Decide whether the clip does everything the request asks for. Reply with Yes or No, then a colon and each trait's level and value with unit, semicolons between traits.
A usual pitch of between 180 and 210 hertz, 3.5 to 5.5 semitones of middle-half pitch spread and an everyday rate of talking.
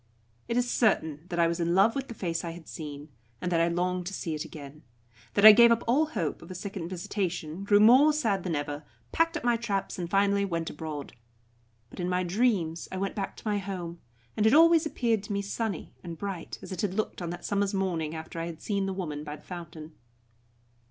No: medium, 185 Hz; average, 3.9 semitones; fast, 230 wpm